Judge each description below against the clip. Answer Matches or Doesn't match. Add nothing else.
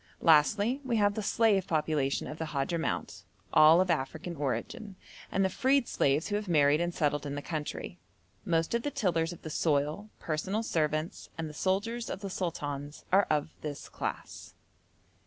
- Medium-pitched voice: Matches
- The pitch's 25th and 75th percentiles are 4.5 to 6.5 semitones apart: Matches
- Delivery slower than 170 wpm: Doesn't match